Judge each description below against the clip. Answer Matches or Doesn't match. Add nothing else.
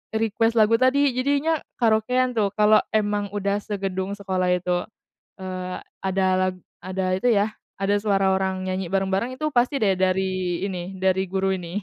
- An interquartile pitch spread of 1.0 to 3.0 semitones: Matches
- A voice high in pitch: Matches